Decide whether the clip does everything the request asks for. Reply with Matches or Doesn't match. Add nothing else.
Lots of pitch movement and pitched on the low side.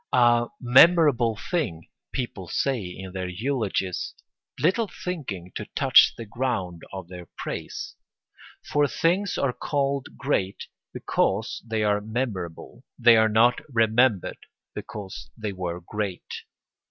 Matches